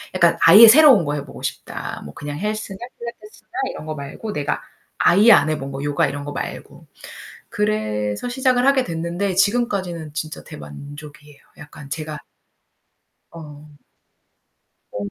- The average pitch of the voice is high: No, medium, 160 Hz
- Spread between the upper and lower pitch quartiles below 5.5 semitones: No, wide, 6.6 semitones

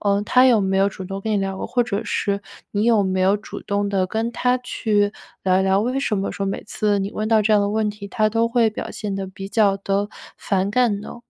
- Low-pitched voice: No, high, 205 Hz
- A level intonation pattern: Yes, narrow, 2.0 semitones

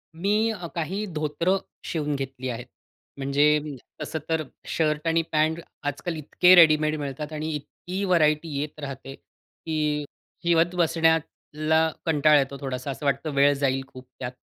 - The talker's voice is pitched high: No, medium, 155 Hz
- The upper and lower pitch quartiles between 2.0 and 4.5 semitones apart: Yes, narrow, 2.6 semitones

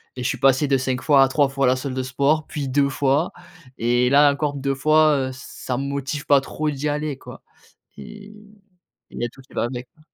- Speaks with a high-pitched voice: No, medium, 140 Hz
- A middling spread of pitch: No, narrow, 1.9 semitones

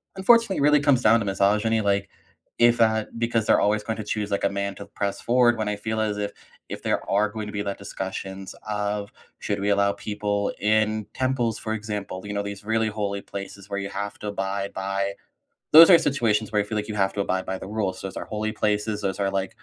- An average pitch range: No, narrow, 1.7 semitones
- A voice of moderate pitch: No, low, 105 Hz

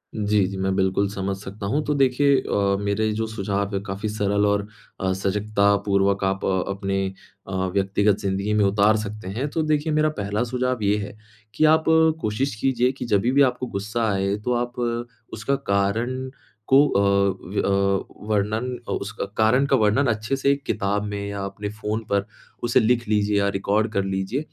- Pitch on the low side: Yes, low, 105 Hz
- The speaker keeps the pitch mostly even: No, average, 3.3 semitones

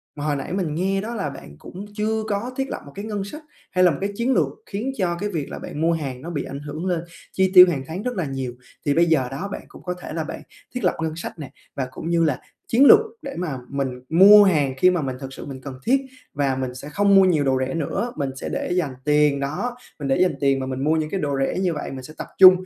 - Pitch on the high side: No, medium, 160 Hz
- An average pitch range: No, wide, 5.7 semitones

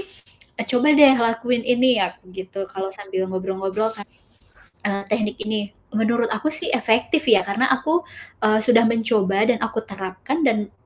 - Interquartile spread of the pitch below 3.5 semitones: No, average, 3.8 semitones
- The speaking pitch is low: No, high, 220 Hz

